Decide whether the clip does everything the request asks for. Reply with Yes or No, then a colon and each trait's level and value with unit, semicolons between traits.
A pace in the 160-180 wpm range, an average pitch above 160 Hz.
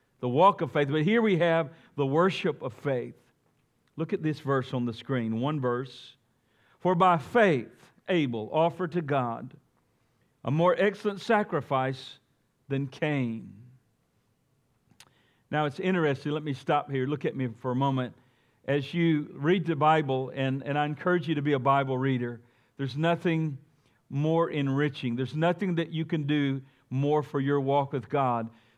No: average, 165 wpm; medium, 140 Hz